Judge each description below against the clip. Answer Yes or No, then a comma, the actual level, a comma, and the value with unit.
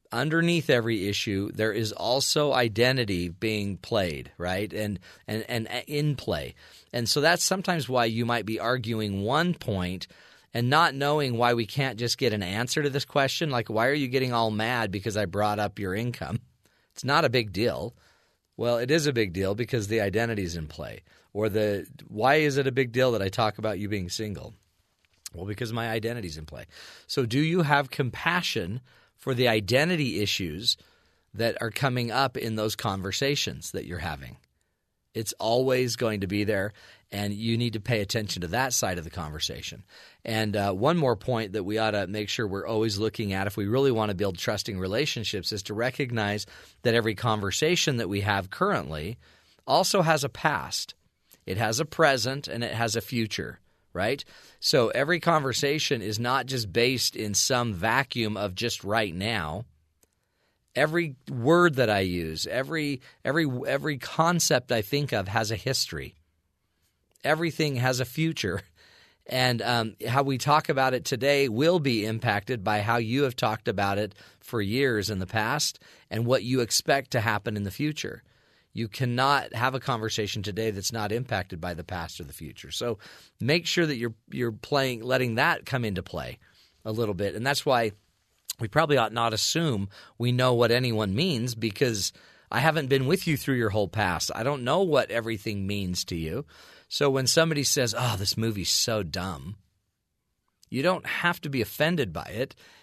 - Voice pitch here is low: Yes, low, 115 Hz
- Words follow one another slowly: No, average, 185 wpm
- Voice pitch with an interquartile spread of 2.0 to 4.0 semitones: No, average, 4.6 semitones